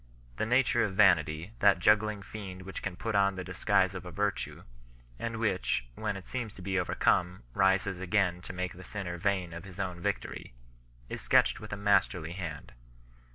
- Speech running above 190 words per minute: Yes, average, 200 wpm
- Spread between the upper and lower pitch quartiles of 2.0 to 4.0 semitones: Yes, narrow, 2.4 semitones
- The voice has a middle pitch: No, very low, 95 Hz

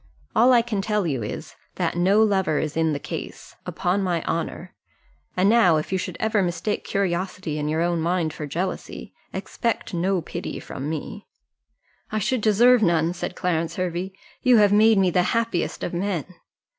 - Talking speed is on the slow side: No, average, 180 wpm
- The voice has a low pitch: No, medium, 185 Hz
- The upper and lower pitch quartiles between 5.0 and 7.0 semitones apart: No, average, 3.9 semitones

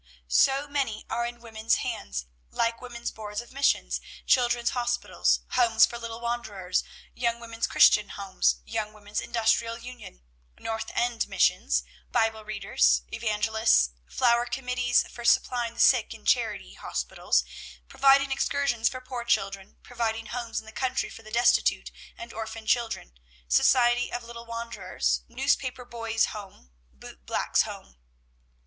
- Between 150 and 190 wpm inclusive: No, average, 140 wpm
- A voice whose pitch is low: No, high, 230 Hz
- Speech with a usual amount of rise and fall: No, narrow, 1.9 semitones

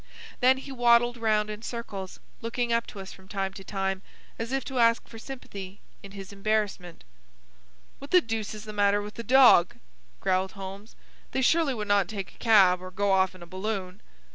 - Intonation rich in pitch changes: No, average, 3.3 semitones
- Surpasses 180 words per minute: Yes, average, 195 wpm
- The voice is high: Yes, high, 210 Hz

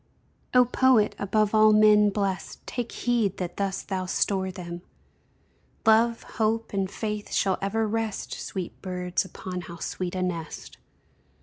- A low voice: No, high, 200 Hz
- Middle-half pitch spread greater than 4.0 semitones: No, average, 3.0 semitones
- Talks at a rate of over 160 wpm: No, average, 140 wpm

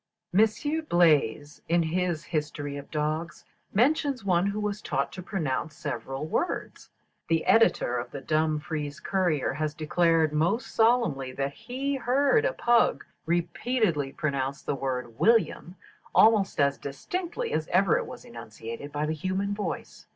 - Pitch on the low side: No, medium, 165 Hz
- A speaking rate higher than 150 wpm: No, average, 145 wpm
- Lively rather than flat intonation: Yes, wide, 7.1 semitones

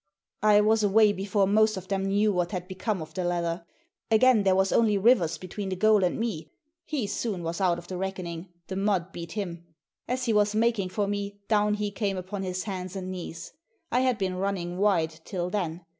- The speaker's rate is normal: No, fast, 210 wpm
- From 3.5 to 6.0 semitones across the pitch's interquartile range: No, narrow, 2.6 semitones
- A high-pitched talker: Yes, high, 195 Hz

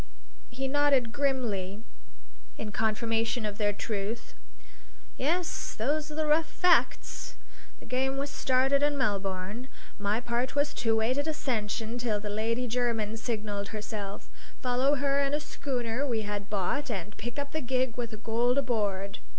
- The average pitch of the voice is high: Yes, high, 240 Hz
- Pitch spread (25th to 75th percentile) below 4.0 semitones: No, average, 4.4 semitones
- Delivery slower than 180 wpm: Yes, average, 155 wpm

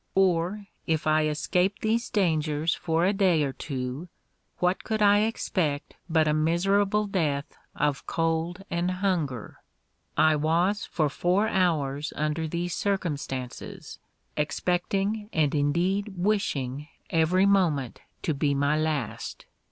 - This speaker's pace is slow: Yes, slow, 125 wpm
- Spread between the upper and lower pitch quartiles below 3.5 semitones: No, average, 4.3 semitones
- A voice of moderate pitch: Yes, medium, 165 Hz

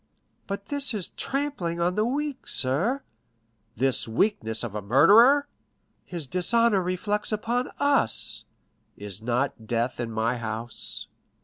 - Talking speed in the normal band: No, slow, 125 wpm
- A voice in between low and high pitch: Yes, medium, 180 Hz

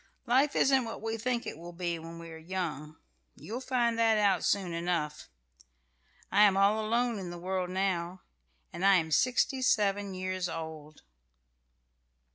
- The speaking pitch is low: No, high, 190 Hz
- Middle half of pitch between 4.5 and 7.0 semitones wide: Yes, average, 4.9 semitones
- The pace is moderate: Yes, average, 160 wpm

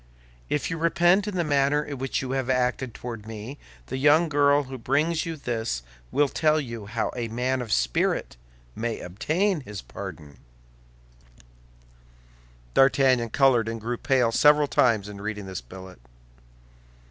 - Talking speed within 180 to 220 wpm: No, average, 150 wpm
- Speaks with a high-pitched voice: No, low, 130 Hz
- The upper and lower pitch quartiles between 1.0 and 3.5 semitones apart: No, average, 4.7 semitones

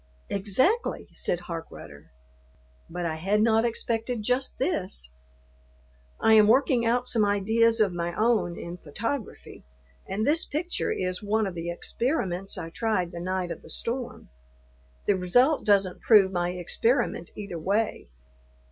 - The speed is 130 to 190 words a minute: Yes, average, 140 wpm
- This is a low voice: No, high, 205 Hz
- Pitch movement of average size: Yes, average, 4.6 semitones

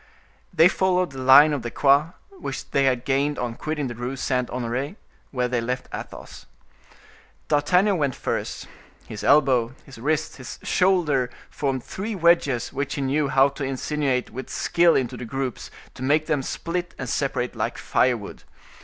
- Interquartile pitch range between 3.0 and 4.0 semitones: Yes, average, 3.3 semitones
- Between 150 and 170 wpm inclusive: Yes, average, 165 wpm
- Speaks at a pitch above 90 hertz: Yes, low, 135 Hz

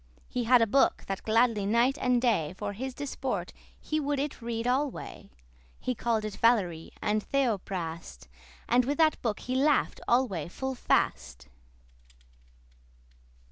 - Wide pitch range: No, average, 4.7 semitones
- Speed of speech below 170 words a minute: Yes, average, 140 wpm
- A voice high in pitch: Yes, high, 235 Hz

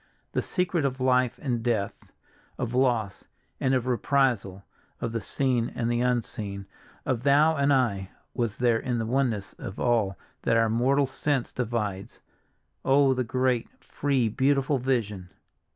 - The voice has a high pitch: No, low, 125 Hz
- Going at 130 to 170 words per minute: Yes, average, 145 wpm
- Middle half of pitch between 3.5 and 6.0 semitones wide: No, average, 2.9 semitones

